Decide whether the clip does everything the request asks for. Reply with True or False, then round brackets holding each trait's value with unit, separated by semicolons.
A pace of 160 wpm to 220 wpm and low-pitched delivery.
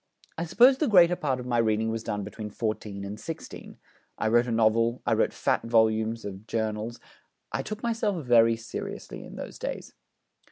True (185 wpm; 115 Hz)